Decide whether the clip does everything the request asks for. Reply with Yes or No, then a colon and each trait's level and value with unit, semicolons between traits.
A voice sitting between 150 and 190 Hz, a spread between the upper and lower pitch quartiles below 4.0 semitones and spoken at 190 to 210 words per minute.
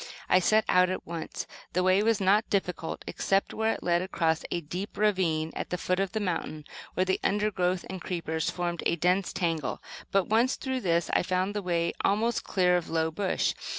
Yes: medium, 185 Hz; narrow, 2.6 semitones; average, 200 wpm